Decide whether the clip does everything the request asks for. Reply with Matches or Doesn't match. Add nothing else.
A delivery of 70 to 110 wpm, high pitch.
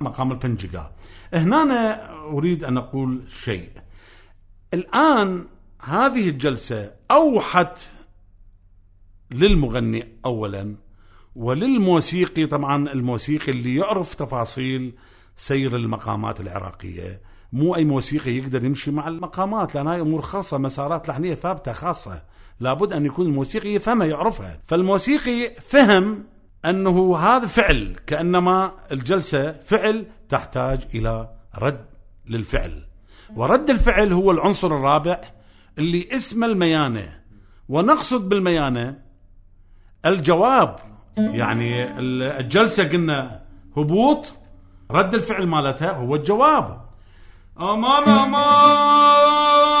Doesn't match